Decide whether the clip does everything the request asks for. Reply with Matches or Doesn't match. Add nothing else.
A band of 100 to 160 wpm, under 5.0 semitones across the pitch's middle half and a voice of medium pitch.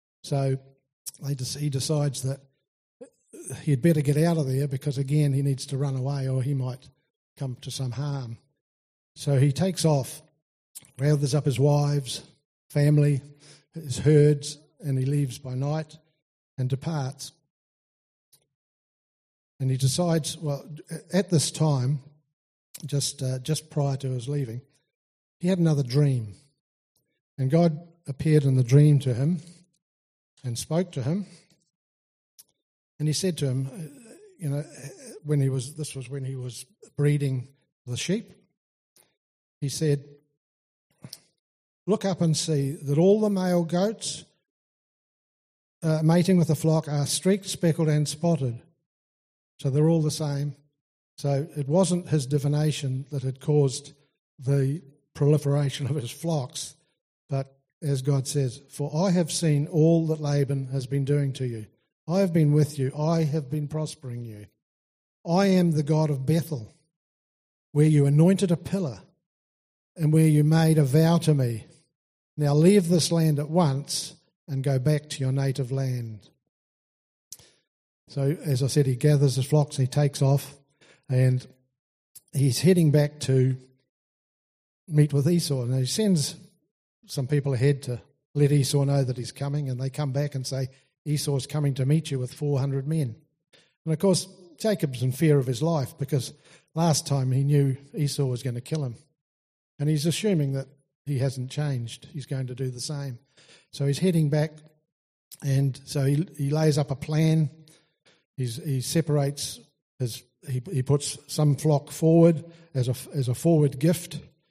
Matches